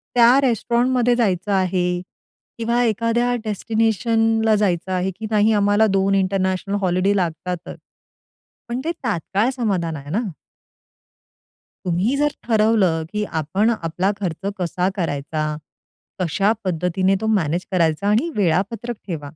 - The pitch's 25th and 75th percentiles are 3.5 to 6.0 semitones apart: Yes, average, 3.9 semitones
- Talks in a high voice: Yes, high, 195 Hz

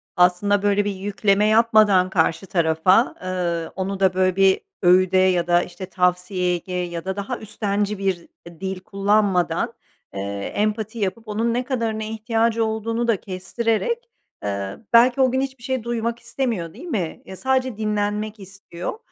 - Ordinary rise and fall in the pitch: Yes, average, 3.7 semitones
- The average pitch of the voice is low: No, high, 200 Hz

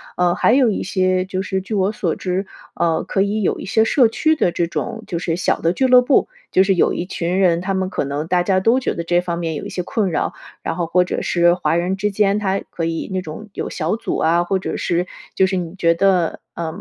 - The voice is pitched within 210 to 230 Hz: No, medium, 185 Hz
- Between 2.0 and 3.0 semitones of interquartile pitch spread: Yes, narrow, 2.5 semitones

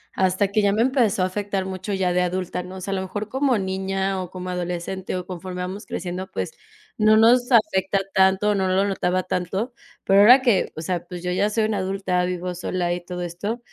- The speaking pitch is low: No, high, 190 Hz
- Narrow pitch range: Yes, narrow, 2.2 semitones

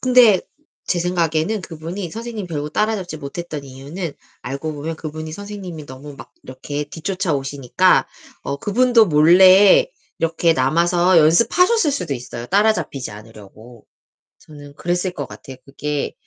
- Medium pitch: Yes, medium, 165 Hz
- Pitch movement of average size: Yes, average, 5.0 semitones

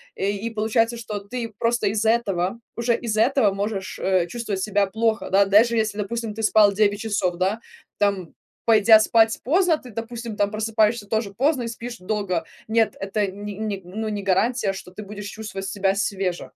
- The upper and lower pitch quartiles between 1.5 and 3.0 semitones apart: Yes, narrow, 2.4 semitones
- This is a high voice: Yes, high, 215 Hz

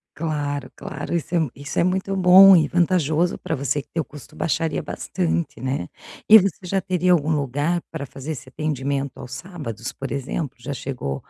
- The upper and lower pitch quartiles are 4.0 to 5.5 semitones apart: Yes, average, 4.3 semitones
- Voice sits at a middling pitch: Yes, medium, 150 Hz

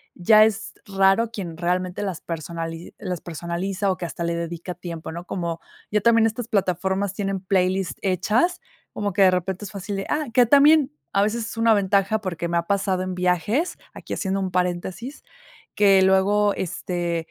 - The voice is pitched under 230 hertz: Yes, high, 190 Hz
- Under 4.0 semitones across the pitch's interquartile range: Yes, average, 2.8 semitones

